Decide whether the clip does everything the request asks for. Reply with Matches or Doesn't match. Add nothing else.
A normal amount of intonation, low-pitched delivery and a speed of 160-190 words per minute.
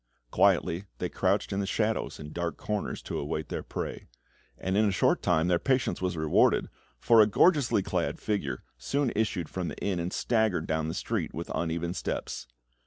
Matches